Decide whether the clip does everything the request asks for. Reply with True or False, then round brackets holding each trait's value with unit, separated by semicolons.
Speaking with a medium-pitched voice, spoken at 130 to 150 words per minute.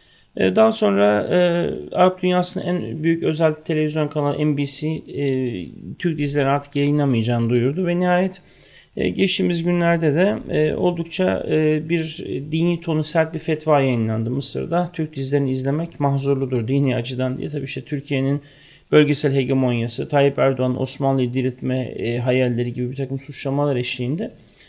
True (145 Hz; 140 wpm)